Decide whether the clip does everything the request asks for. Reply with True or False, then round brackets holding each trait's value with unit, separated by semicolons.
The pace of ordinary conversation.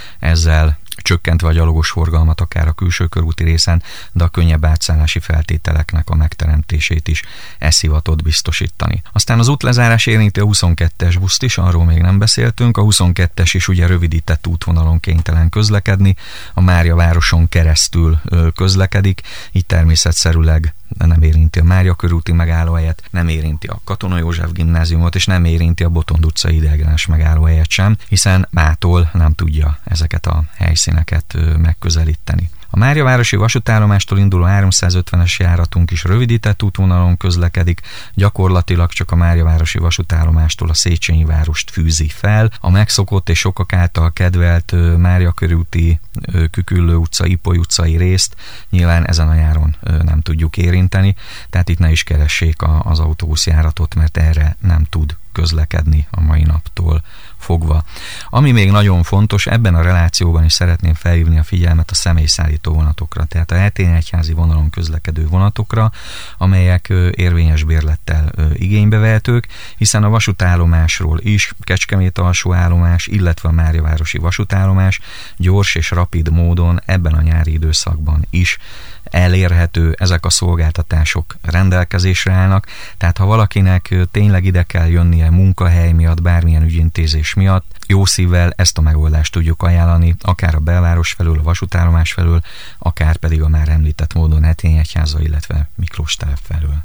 True (140 wpm)